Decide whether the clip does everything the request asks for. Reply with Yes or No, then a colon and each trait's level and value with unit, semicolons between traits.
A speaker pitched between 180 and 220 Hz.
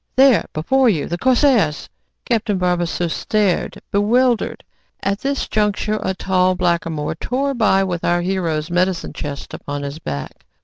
Yes: medium, 185 Hz